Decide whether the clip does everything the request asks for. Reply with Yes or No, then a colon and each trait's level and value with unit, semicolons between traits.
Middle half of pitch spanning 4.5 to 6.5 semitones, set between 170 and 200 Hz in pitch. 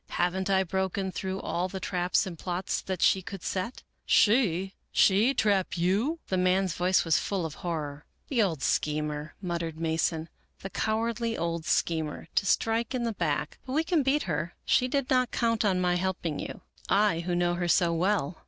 No: average, 3.8 semitones; medium, 185 Hz